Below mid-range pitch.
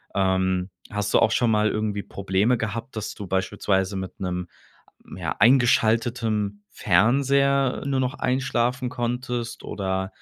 Yes: low, 110 Hz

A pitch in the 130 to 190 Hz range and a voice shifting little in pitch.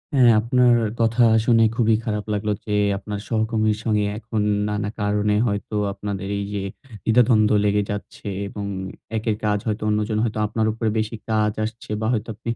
No: low, 110 Hz; narrow, 1.4 semitones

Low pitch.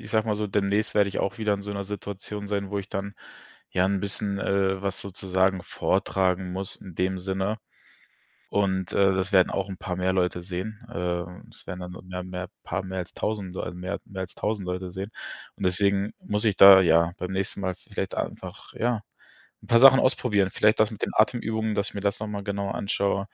Yes: low, 100 Hz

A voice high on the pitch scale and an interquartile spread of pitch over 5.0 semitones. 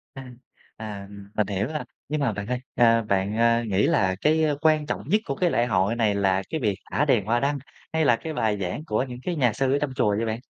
No: low, 115 Hz; wide, 5.4 semitones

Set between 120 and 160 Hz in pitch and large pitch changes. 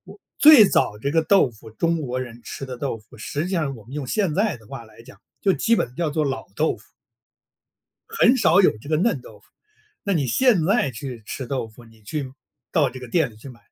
Yes: medium, 140 Hz; wide, 6.4 semitones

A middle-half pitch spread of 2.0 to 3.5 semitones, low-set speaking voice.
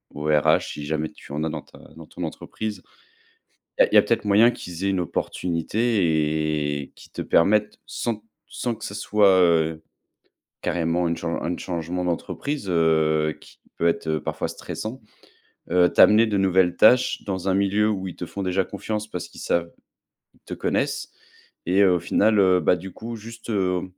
No: average, 4.0 semitones; very low, 90 Hz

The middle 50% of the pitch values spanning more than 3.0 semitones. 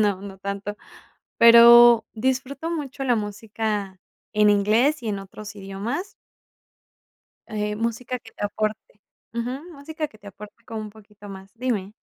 No: average, 2.7 semitones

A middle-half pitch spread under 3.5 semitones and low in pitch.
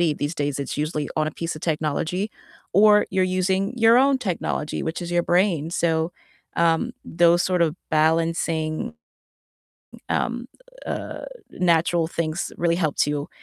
No: average, 2.8 semitones; medium, 170 Hz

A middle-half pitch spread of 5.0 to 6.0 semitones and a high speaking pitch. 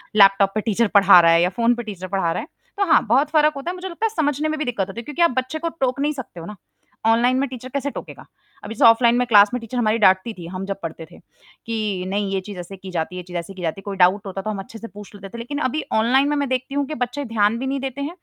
Yes: wide, 5.6 semitones; high, 225 Hz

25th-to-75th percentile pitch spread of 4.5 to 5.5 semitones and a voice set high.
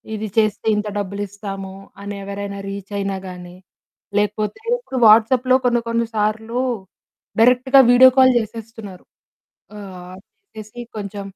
No: narrow, 2.6 semitones; high, 210 Hz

